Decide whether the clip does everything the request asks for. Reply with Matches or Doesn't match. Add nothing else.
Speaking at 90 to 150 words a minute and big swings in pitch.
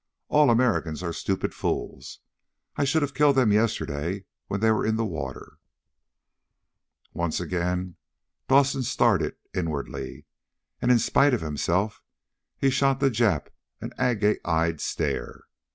Matches